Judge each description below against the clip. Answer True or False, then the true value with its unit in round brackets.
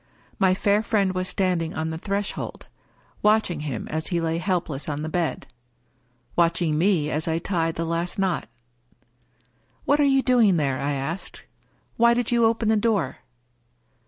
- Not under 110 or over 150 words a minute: False (180 wpm)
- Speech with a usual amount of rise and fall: True (4.5 semitones)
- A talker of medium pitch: True (175 Hz)